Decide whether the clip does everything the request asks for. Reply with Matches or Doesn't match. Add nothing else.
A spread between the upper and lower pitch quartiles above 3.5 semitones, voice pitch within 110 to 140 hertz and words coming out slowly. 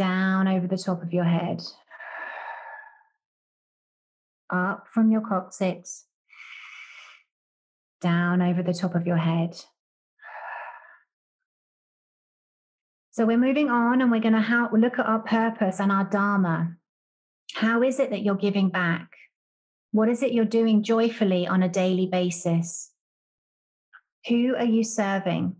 Doesn't match